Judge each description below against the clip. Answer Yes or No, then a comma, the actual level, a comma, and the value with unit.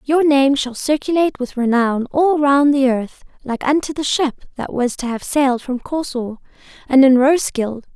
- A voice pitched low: No, very high, 270 Hz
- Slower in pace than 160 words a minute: No, average, 180 wpm